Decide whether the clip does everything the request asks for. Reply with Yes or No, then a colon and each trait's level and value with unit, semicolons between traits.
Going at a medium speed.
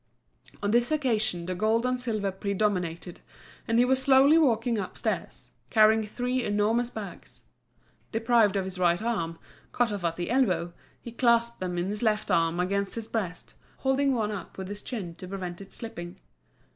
Yes: average, 170 wpm